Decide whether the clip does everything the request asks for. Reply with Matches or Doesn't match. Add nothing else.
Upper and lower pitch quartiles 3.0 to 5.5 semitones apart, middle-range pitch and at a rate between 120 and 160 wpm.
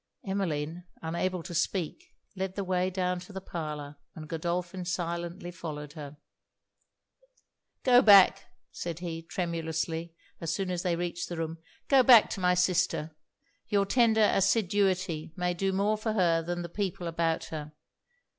Doesn't match